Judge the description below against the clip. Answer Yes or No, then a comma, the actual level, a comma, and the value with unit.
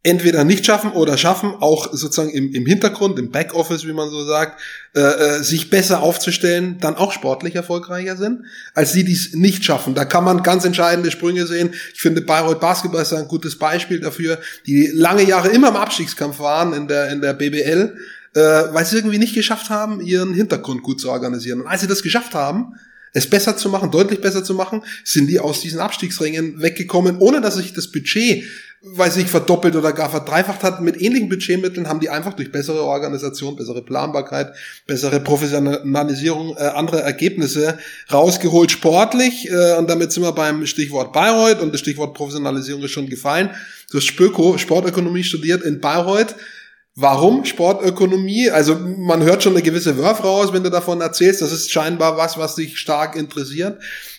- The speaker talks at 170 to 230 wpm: Yes, average, 180 wpm